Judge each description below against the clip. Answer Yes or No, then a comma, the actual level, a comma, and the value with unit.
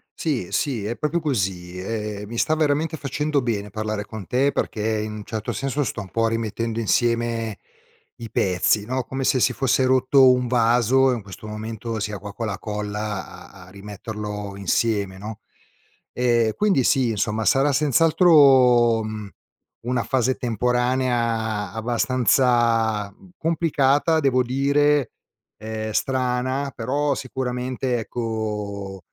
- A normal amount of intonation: Yes, average, 3.6 semitones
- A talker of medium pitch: No, low, 115 Hz